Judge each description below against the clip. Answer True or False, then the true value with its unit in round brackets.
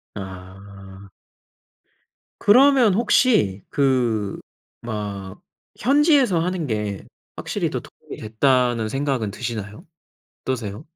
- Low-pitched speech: True (115 Hz)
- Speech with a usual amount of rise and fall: False (8.5 semitones)